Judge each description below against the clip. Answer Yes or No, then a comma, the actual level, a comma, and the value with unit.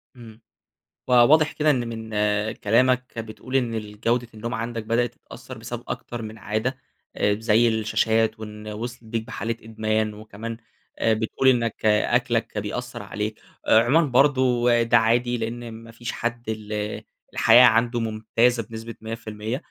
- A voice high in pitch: No, low, 115 Hz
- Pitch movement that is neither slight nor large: No, narrow, 1.7 semitones